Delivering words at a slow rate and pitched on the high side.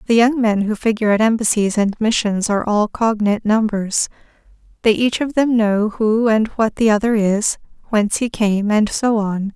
No: average, 190 wpm; high, 215 Hz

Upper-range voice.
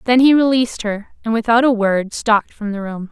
Yes: high, 225 Hz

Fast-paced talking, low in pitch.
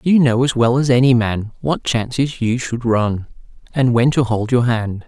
Yes: fast, 215 wpm; low, 120 Hz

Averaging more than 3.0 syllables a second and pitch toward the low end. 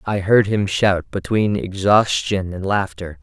Yes: 4.0 syllables/s; very low, 95 Hz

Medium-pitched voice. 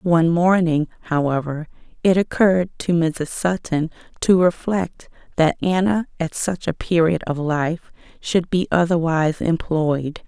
Yes: medium, 170 Hz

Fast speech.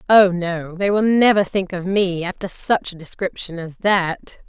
No: average, 190 wpm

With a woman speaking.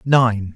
No: male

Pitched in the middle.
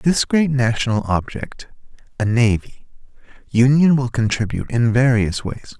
No: low, 120 Hz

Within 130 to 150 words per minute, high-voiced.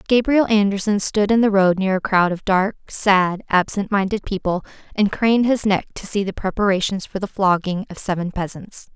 No: average, 195 wpm; high, 195 Hz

